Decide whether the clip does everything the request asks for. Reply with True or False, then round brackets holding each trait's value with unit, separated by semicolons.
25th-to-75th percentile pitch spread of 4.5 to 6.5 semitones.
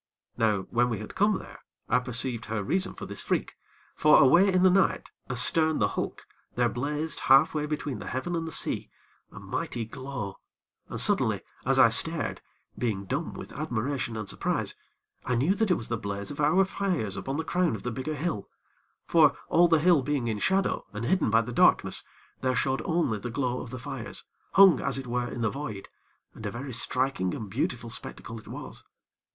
True (5.6 semitones)